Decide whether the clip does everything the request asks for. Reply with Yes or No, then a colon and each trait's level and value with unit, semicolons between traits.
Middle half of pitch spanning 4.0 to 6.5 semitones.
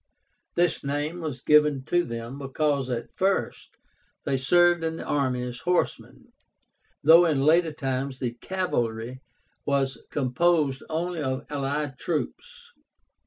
Yes: average, 4.3 semitones